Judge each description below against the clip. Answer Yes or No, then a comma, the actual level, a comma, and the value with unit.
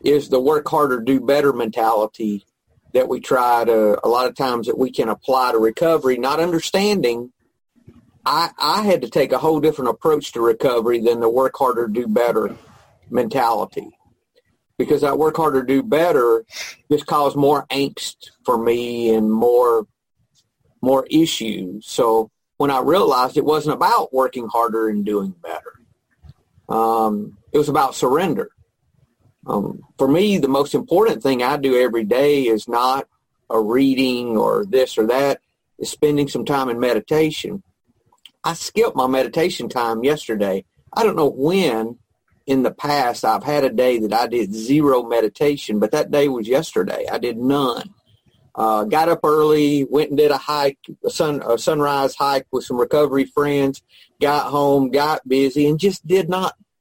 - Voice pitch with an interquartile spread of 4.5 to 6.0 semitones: No, average, 4.0 semitones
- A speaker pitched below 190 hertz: Yes, low, 135 Hz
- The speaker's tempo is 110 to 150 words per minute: No, average, 165 wpm